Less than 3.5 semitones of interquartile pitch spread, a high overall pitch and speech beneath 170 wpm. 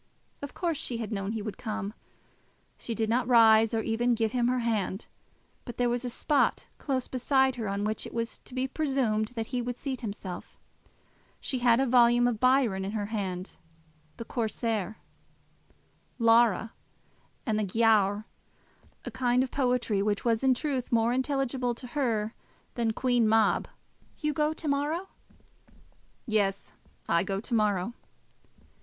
Yes: average, 2.9 semitones; high, 235 Hz; average, 160 wpm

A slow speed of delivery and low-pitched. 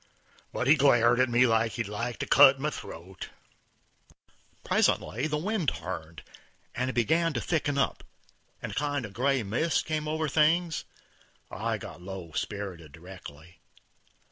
No: average, 145 wpm; low, 125 Hz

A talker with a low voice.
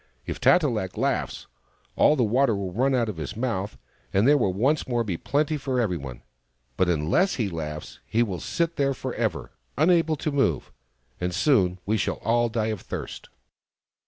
Yes: low, 115 Hz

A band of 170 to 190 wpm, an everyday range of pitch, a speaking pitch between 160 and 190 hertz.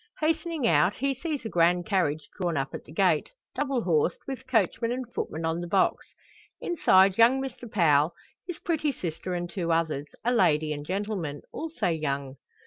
No: average, 175 wpm; wide, 8.1 semitones; medium, 185 Hz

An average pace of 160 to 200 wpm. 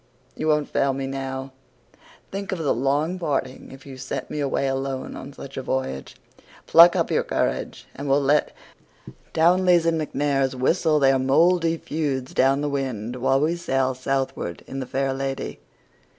Yes: average, 165 wpm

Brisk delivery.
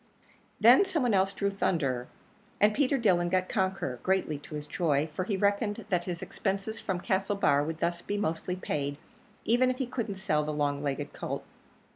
No: average, 185 wpm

